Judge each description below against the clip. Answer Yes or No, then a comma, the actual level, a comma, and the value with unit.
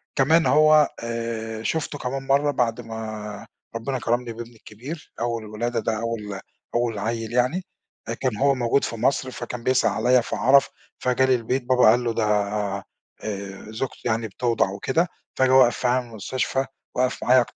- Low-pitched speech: Yes, low, 120 Hz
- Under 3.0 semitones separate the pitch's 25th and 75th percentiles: Yes, narrow, 2.6 semitones